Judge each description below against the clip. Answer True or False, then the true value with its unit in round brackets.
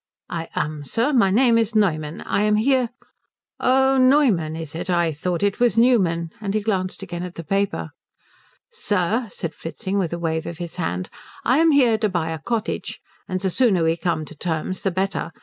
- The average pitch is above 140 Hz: True (190 Hz)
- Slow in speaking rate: False (200 wpm)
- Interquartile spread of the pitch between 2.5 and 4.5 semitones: False (5.5 semitones)